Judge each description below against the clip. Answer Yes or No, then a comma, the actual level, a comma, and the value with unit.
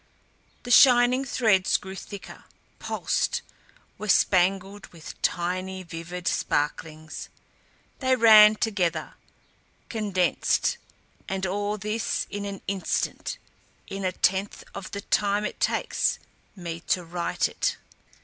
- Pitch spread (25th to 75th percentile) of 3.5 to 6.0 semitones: No, average, 2.8 semitones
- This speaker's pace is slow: Yes, slow, 110 wpm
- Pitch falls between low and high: No, high, 195 Hz